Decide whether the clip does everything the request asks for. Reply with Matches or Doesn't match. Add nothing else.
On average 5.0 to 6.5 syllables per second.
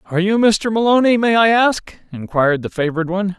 Matches